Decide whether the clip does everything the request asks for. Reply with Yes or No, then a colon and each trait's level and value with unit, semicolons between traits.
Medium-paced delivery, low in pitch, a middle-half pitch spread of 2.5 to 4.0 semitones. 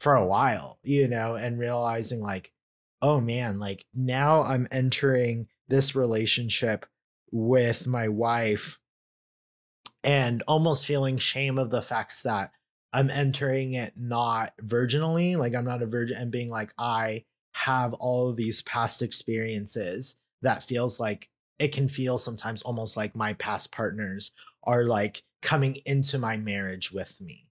Yes: average, 145 wpm; low, 120 Hz; average, 2.9 semitones